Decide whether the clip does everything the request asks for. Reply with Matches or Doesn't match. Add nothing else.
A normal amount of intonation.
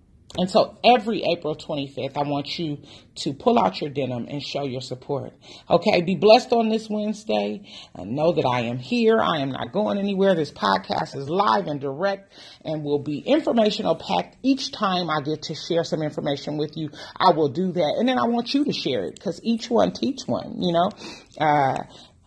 Doesn't match